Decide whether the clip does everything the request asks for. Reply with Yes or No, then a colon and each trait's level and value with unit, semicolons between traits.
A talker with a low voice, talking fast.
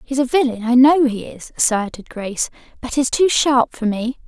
No: very high, 250 Hz; fast, 210 wpm